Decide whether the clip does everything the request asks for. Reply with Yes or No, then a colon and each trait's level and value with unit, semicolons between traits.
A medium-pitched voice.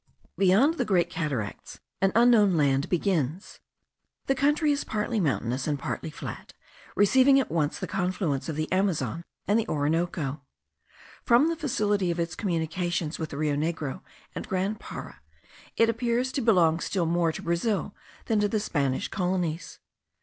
Yes: medium, 180 Hz